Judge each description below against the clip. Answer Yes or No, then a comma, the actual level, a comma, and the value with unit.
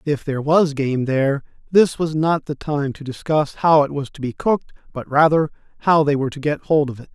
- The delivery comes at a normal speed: No, fast, 235 wpm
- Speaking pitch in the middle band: Yes, medium, 145 Hz